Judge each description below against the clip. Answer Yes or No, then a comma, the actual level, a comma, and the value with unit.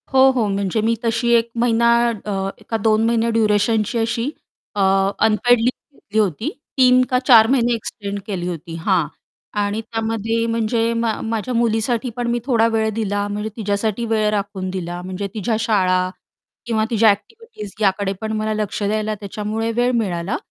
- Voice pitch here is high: Yes, high, 220 Hz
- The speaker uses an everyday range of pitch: No, narrow, 2.2 semitones